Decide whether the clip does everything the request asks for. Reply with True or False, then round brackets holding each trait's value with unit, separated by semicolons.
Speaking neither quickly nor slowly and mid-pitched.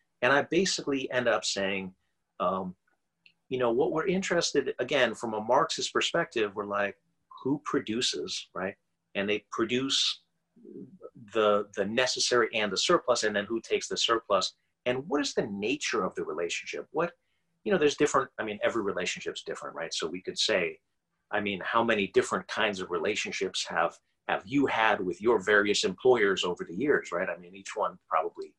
True (180 wpm; 175 Hz)